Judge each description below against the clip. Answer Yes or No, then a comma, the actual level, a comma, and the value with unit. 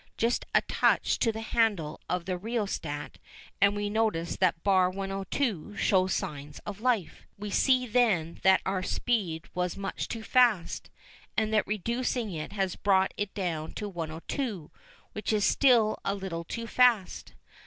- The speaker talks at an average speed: Yes, average, 160 wpm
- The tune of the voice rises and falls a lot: No, average, 3.7 semitones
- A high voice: Yes, high, 200 Hz